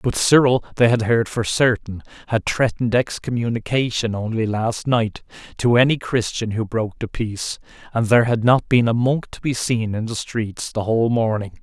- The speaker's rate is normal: Yes, average, 185 wpm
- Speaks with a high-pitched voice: No, low, 115 Hz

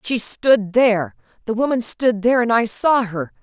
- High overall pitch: Yes, high, 225 Hz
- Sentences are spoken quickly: No, average, 195 wpm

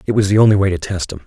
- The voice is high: No, very low, 95 Hz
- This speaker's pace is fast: Yes, fast, 380 wpm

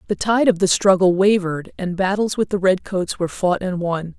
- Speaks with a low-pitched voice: No, high, 190 Hz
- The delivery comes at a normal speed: No, fast, 230 wpm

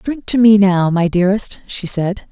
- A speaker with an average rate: No, fast, 210 wpm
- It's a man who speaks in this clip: No, female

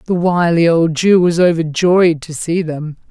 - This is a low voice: No, medium, 170 Hz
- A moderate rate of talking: Yes, average, 175 wpm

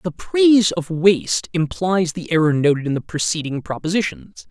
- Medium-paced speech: Yes, average, 160 wpm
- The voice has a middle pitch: Yes, medium, 165 Hz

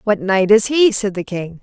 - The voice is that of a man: No, female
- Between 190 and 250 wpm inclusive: No, fast, 260 wpm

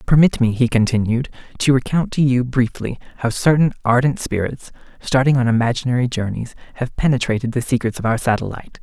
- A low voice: Yes, low, 125 Hz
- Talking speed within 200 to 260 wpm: No, average, 165 wpm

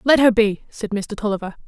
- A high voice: Yes, high, 215 Hz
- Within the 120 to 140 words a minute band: No, fast, 215 wpm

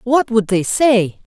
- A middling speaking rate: Yes, average, 180 wpm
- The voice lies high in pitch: Yes, high, 225 Hz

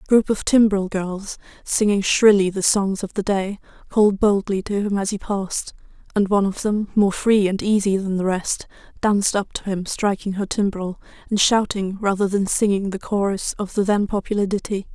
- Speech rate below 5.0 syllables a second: No, 5.1 syllables/s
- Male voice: No, female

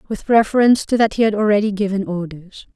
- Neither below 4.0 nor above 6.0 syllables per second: No, 6.4 syllables/s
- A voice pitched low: No, high, 205 Hz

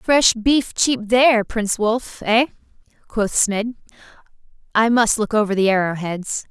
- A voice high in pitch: Yes, high, 220 Hz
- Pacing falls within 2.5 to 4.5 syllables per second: Yes, 4.2 syllables/s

